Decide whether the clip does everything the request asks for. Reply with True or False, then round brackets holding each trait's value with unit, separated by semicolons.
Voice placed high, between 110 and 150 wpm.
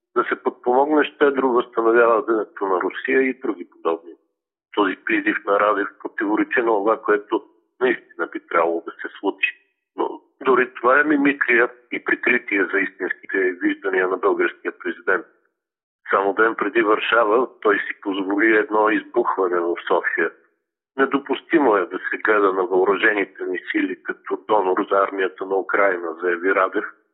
True (345 Hz; 145 wpm)